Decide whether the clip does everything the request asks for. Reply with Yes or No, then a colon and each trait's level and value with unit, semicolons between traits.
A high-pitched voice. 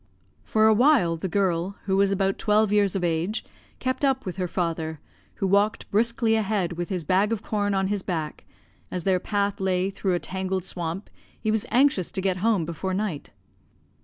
Yes: high, 195 Hz